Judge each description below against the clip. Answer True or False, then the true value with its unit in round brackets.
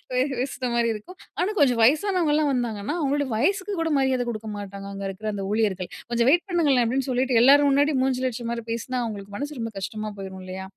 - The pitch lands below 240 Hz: False (245 Hz)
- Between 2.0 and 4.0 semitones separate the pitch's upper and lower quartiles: False (5.1 semitones)